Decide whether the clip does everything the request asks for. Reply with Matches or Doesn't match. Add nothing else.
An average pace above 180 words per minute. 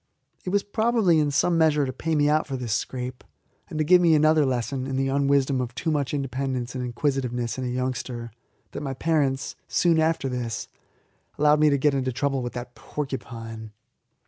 Matches